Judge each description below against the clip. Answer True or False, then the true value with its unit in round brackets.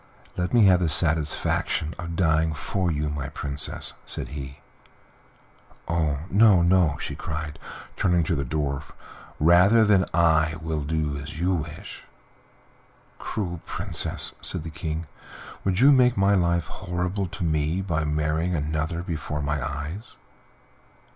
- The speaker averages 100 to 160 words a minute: True (140 wpm)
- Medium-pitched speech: False (80 Hz)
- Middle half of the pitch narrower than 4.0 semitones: True (3.0 semitones)